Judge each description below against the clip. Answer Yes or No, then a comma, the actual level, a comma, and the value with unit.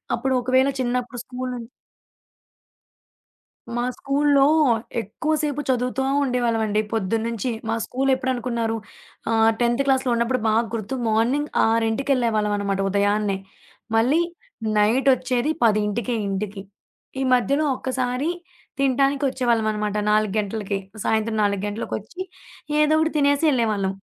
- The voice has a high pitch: Yes, high, 240 Hz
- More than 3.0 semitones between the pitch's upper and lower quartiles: Yes, average, 3.5 semitones